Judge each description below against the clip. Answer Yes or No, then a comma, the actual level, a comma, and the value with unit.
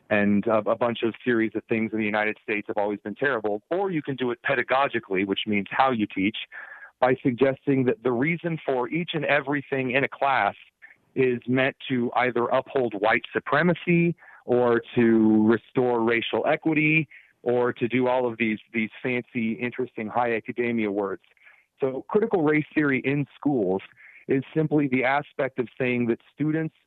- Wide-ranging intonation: No, average, 3.7 semitones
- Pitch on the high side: No, low, 125 Hz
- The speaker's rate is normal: Yes, average, 170 wpm